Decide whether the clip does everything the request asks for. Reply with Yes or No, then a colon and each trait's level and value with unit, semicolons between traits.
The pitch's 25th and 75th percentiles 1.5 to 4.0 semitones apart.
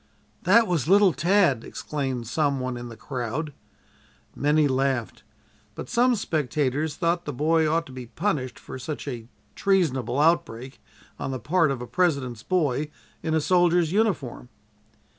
No: average, 5.1 semitones